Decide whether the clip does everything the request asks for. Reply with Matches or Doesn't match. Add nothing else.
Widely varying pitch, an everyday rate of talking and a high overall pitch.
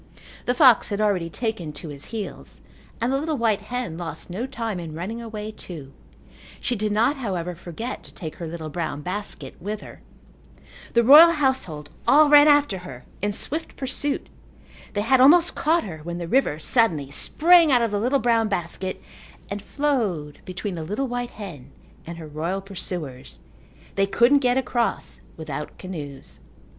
Matches